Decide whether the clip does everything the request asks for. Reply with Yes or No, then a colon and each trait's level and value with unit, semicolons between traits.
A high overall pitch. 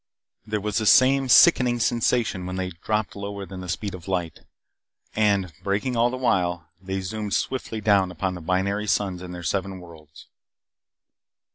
No: low, 100 Hz